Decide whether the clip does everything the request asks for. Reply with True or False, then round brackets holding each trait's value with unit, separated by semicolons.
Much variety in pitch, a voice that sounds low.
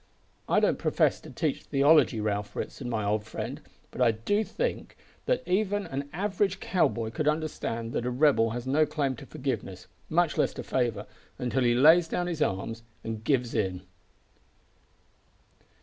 True (6.0 semitones; 130 Hz)